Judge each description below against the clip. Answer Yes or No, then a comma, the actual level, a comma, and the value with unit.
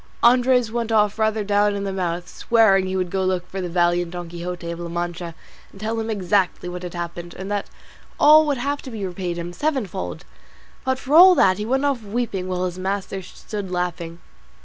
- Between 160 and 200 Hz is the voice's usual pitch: Yes, high, 190 Hz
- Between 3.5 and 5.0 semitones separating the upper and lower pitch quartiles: Yes, average, 4.1 semitones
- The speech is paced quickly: Yes, fast, 215 wpm